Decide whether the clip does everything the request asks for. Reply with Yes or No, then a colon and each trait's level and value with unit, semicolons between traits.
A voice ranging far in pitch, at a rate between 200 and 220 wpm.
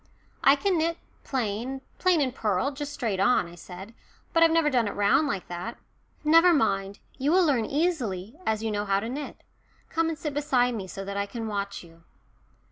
Yes: wide, 6.9 semitones; fast, 205 wpm